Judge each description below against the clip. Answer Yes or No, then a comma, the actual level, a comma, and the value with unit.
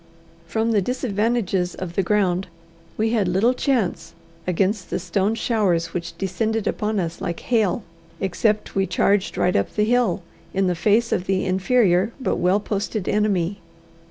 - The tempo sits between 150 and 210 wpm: Yes, average, 155 wpm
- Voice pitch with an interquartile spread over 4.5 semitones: No, average, 3.3 semitones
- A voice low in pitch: No, high, 200 Hz